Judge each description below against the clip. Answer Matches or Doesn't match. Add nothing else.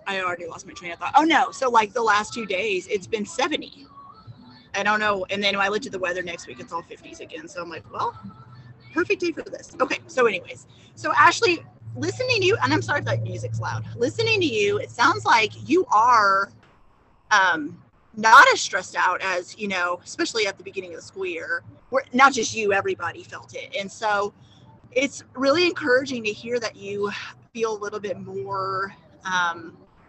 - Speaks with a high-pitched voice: Matches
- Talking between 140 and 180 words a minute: Doesn't match